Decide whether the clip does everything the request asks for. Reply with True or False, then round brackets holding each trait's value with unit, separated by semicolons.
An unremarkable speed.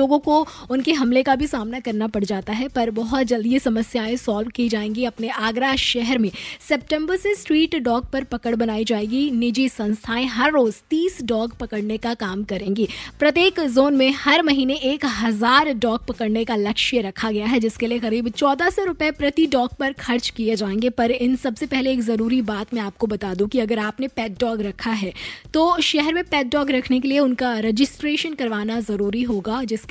False (195 wpm)